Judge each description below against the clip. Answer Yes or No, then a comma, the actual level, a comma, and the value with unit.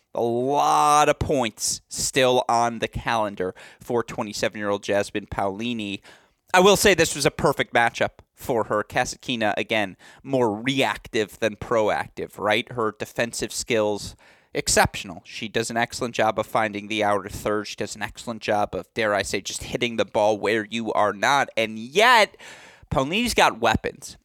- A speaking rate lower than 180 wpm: Yes, average, 165 wpm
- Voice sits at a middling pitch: No, low, 115 Hz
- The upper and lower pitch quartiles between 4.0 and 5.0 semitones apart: No, average, 2.9 semitones